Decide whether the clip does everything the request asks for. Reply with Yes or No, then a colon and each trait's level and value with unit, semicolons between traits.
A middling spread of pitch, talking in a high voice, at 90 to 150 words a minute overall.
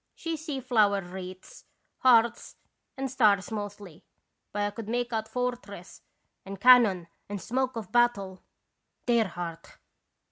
Yes: average, 4.0 semitones; high, 215 Hz; slow, 135 wpm